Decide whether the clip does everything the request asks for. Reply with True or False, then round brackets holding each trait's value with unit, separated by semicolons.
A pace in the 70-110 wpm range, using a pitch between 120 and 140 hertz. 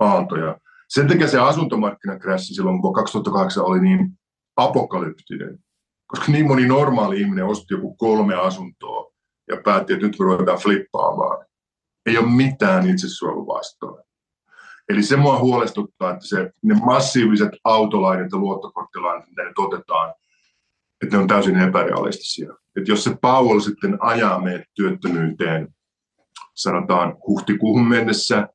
False (130 wpm; 125 Hz)